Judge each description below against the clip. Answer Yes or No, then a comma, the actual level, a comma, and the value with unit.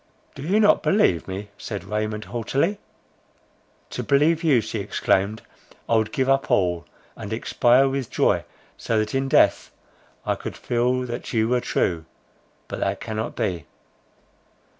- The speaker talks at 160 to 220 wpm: No, average, 145 wpm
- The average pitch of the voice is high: No, low, 115 Hz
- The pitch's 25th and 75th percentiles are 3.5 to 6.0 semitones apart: Yes, average, 4.2 semitones